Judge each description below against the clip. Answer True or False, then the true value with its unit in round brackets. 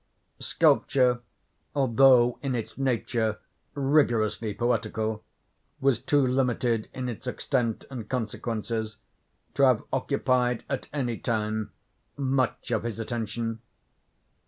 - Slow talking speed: True (105 wpm)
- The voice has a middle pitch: False (120 Hz)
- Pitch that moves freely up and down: False (2.9 semitones)